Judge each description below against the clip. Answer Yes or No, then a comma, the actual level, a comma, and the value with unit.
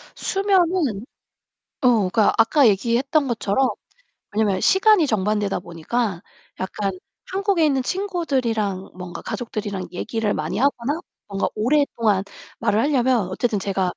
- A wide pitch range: Yes, wide, 6.3 semitones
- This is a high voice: Yes, high, 230 Hz